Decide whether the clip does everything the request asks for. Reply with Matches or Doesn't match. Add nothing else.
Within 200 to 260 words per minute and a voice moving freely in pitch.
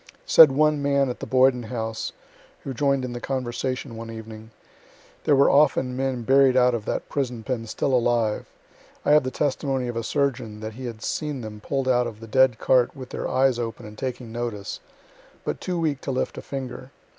Doesn't match